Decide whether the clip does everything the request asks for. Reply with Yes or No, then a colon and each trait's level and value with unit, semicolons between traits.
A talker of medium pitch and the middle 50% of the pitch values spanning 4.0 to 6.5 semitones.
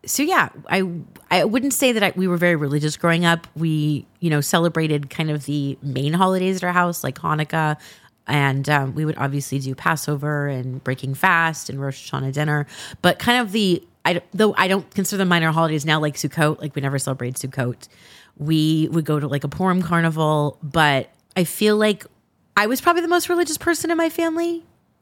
Yes: medium, 160 Hz; average, 4.4 semitones